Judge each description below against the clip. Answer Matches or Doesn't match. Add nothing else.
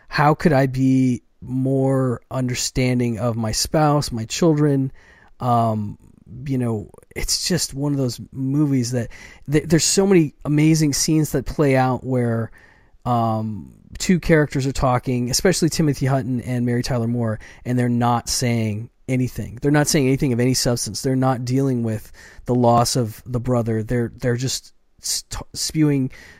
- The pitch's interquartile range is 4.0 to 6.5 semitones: Doesn't match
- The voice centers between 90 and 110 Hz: Doesn't match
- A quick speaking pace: Doesn't match